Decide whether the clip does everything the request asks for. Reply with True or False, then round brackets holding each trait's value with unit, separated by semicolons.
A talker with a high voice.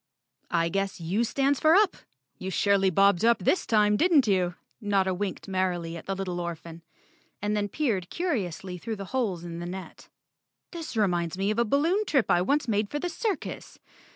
True (200 Hz)